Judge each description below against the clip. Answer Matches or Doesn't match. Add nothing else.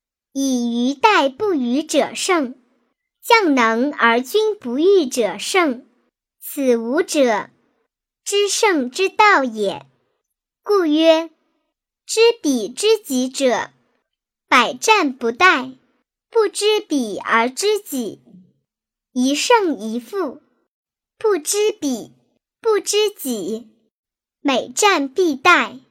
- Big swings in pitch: Matches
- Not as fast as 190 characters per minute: Matches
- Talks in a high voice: Matches